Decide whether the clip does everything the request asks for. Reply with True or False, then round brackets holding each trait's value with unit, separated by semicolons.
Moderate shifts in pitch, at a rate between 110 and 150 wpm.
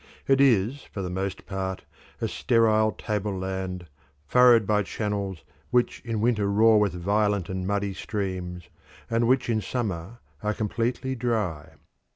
True (3.4 semitones; 140 wpm)